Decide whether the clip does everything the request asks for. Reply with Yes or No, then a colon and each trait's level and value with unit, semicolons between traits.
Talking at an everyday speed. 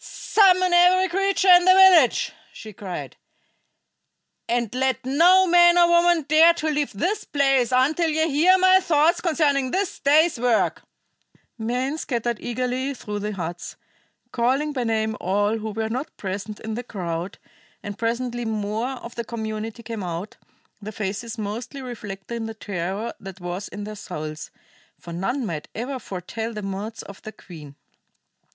Yes: average, 155 wpm